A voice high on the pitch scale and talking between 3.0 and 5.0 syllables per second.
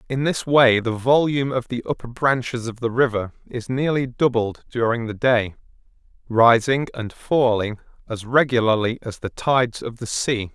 No: low, 120 Hz; 4.8 syllables/s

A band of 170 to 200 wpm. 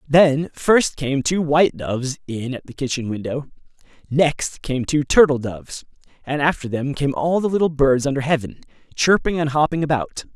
Yes: average, 175 wpm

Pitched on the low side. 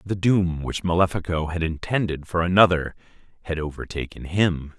Yes: very low, 85 Hz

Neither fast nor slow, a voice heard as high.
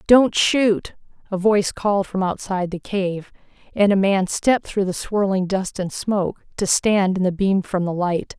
Yes: average, 195 wpm; high, 195 Hz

